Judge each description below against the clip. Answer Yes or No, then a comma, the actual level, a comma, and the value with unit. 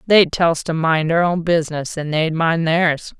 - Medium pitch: Yes, medium, 165 Hz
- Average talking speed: No, fast, 225 wpm